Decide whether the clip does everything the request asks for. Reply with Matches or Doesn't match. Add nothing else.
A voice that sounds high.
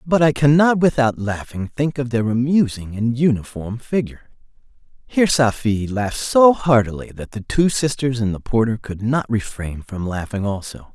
Doesn't match